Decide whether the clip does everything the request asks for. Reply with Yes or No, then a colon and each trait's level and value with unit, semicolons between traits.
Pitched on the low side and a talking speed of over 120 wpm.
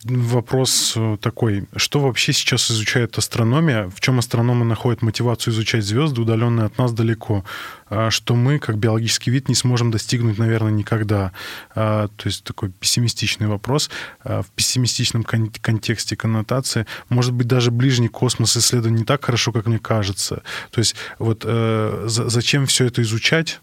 Yes: low, 115 Hz; average, 140 wpm